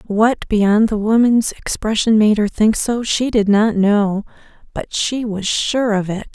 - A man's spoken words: No, female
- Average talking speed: Yes, average, 180 wpm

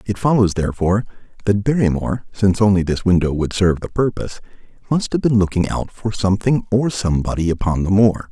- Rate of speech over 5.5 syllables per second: Yes, 6.3 syllables/s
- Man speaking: Yes, male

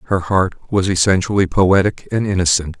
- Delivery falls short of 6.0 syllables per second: Yes, 5.0 syllables/s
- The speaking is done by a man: Yes, male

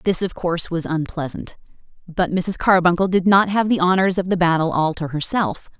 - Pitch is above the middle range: No, medium, 175 Hz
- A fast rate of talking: No, average, 195 wpm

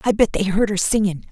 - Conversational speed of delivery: No, fast, 275 wpm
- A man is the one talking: No, female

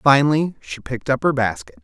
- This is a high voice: No, low, 130 Hz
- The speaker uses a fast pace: No, average, 195 wpm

